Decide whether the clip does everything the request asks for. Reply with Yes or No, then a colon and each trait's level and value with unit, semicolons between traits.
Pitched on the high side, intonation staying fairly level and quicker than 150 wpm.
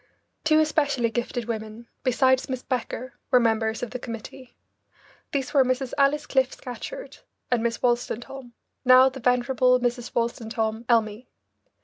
No: very high, 250 Hz; narrow, 2.1 semitones; slow, 135 wpm